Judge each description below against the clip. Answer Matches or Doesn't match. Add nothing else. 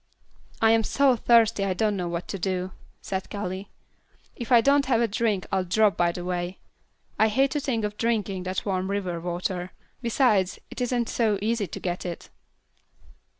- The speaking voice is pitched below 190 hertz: Doesn't match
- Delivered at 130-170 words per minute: Doesn't match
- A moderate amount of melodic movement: Matches